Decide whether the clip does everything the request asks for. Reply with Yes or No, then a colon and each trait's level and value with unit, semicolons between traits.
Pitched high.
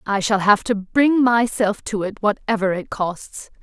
Yes: high, 210 Hz